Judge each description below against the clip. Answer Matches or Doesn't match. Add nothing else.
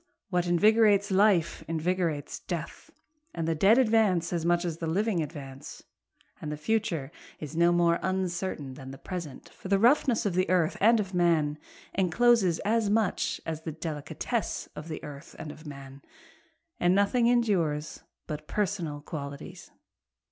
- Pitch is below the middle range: Doesn't match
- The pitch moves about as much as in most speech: Matches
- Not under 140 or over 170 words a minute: Matches